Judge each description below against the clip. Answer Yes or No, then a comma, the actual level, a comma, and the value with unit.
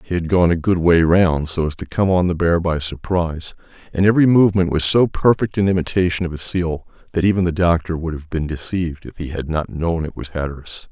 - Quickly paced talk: Yes, fast, 235 wpm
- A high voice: No, very low, 85 Hz